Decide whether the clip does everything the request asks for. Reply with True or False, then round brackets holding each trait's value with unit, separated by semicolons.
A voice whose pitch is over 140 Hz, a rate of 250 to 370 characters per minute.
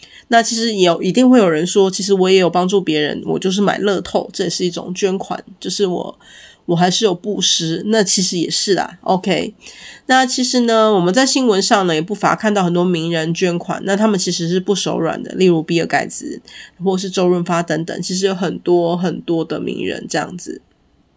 True (185 Hz; 305 characters per minute)